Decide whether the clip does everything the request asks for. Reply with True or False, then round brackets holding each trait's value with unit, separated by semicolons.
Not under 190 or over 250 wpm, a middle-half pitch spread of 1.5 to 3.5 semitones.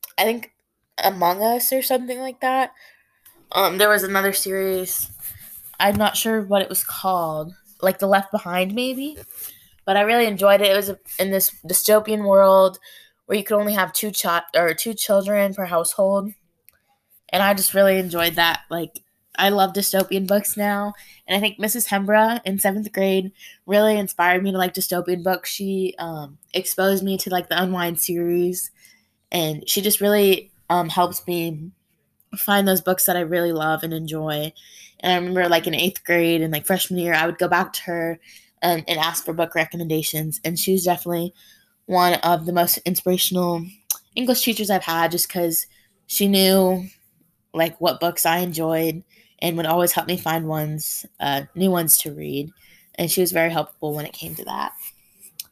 False (180 wpm; 2.9 semitones)